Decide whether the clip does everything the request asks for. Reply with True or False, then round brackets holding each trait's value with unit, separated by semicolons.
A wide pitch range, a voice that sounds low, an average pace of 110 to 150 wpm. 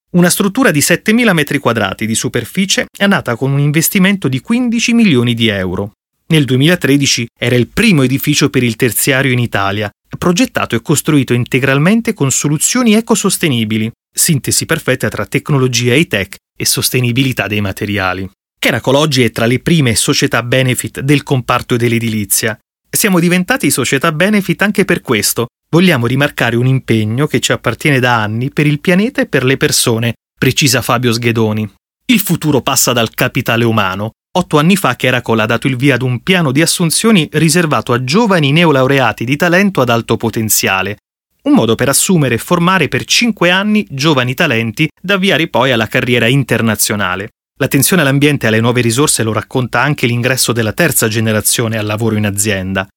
False (6.0 semitones; 130 Hz; 165 wpm)